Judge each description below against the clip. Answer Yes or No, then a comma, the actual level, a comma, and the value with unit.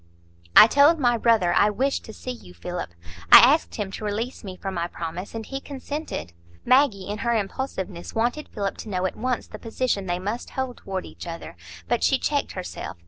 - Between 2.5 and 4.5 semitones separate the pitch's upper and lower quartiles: No, average, 5.2 semitones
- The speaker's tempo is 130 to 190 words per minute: No, average, 200 wpm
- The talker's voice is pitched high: Yes, high, 215 Hz